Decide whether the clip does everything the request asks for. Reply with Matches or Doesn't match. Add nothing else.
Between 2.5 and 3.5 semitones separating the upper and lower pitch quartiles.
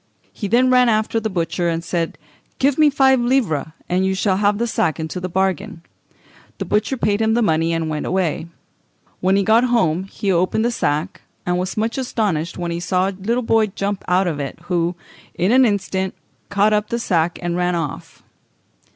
Doesn't match